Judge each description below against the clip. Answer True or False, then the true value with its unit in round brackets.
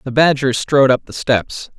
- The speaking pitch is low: True (130 Hz)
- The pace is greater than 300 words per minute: False (200 wpm)